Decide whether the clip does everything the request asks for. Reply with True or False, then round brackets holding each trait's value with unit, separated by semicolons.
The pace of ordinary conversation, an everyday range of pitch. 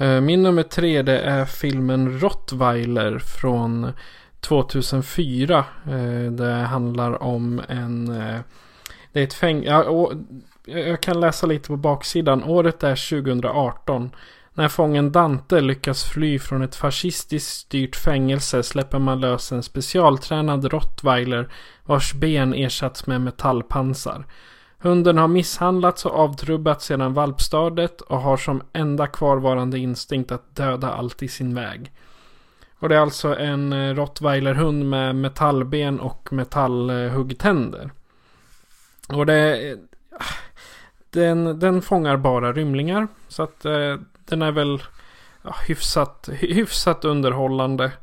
False (110 wpm; 3.1 semitones)